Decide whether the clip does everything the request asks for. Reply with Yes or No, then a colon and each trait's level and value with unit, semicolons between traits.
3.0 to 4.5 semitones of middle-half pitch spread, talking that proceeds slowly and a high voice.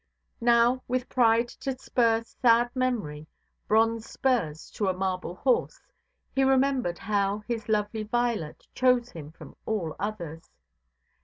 Yes: average, 4.1 semitones; slow, 115 wpm; high, 225 Hz